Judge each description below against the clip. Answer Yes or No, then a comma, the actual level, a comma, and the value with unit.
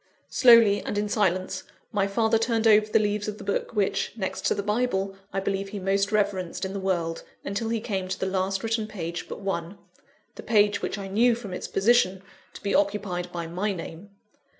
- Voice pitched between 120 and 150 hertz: No, high, 200 Hz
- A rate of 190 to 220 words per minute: Yes, fast, 205 wpm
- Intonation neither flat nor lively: No, narrow, 2.0 semitones